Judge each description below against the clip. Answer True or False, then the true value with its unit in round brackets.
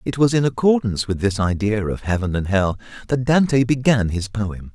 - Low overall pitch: True (110 Hz)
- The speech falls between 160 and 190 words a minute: False (200 wpm)